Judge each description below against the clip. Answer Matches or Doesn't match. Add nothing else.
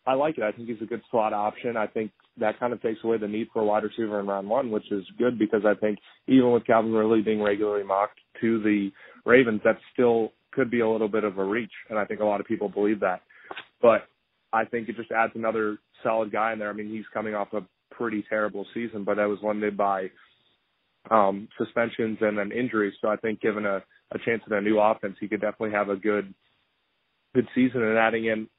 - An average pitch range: Doesn't match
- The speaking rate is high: Matches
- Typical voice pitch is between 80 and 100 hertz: Doesn't match